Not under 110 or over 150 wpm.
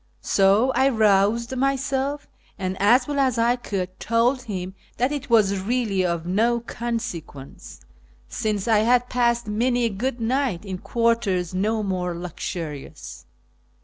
Yes: average, 140 wpm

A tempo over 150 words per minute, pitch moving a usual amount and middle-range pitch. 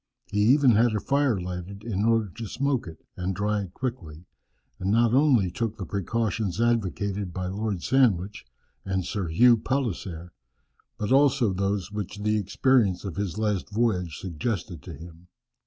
No: average, 160 wpm; average, 4.1 semitones; low, 105 Hz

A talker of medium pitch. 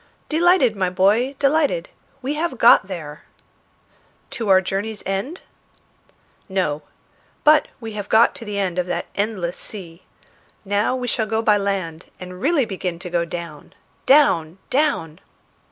No: high, 200 Hz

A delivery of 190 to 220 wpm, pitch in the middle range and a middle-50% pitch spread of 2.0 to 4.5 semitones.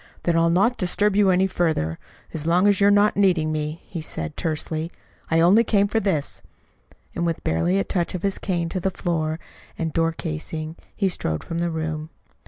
Yes: average, 195 wpm; medium, 170 Hz; average, 3.4 semitones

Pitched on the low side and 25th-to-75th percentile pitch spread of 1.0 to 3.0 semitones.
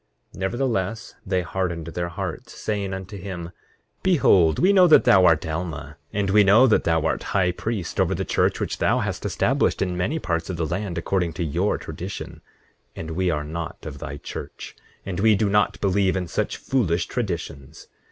No: very low, 95 Hz; average, 3.5 semitones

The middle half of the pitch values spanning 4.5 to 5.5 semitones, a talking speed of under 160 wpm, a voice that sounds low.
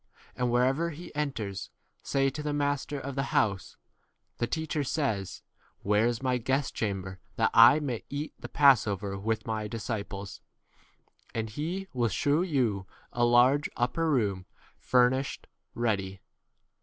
Yes: average, 5.1 semitones; average, 145 wpm; low, 125 Hz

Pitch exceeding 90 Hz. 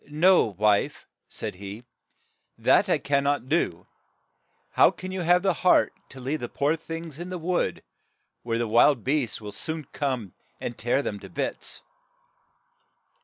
Yes: medium, 140 Hz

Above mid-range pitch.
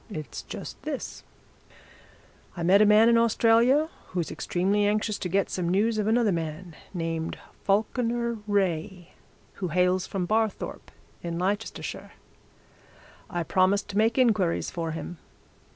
Yes: high, 195 Hz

